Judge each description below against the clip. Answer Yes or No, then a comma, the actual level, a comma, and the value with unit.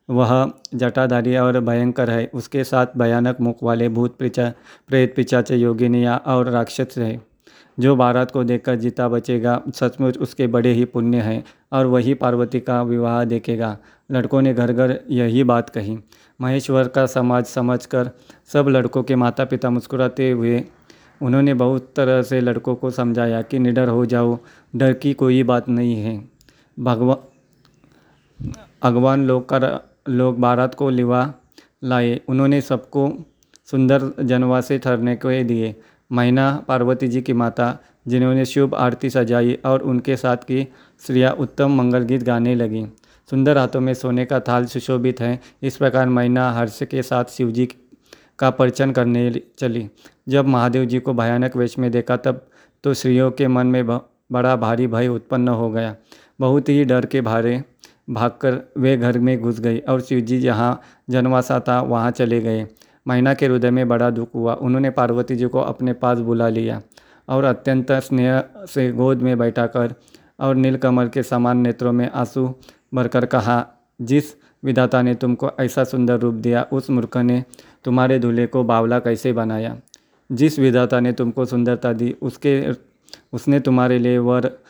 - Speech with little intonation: Yes, narrow, 1.4 semitones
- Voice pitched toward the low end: Yes, low, 125 Hz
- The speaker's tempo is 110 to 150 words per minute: No, average, 160 wpm